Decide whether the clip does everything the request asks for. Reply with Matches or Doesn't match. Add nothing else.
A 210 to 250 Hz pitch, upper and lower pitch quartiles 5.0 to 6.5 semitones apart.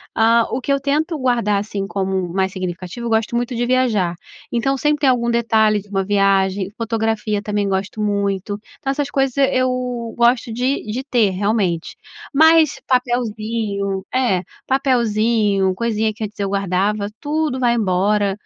Doesn't match